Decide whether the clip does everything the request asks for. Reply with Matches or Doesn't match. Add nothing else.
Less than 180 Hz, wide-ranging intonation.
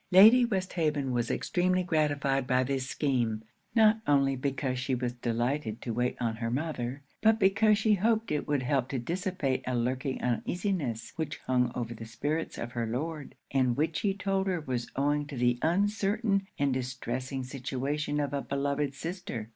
Matches